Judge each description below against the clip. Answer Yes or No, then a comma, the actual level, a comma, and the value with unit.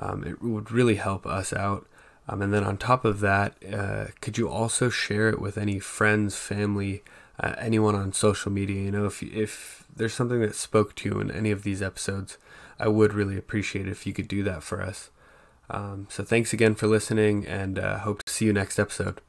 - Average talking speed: No, fast, 220 wpm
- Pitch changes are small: Yes, narrow, 1.7 semitones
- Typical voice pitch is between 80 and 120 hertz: Yes, low, 105 Hz